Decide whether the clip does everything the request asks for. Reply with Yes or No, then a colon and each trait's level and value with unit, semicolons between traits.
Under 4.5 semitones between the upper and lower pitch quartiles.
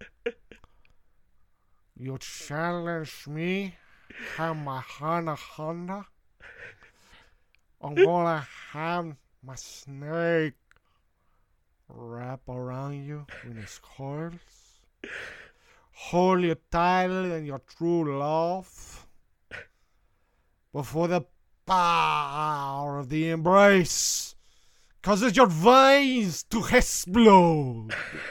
No: average, 5.1 semitones